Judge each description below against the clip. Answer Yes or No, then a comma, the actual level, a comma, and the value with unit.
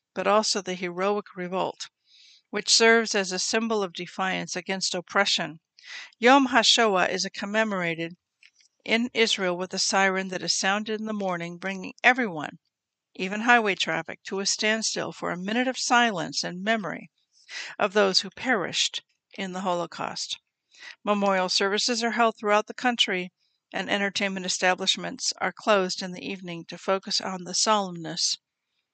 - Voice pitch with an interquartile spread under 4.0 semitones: Yes, average, 3.0 semitones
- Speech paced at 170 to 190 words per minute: No, average, 150 wpm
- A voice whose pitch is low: No, high, 195 Hz